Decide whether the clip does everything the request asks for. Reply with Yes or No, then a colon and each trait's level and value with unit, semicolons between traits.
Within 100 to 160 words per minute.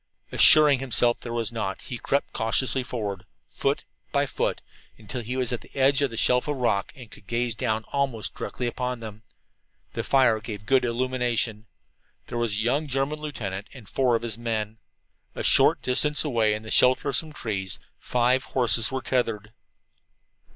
No: average, 180 wpm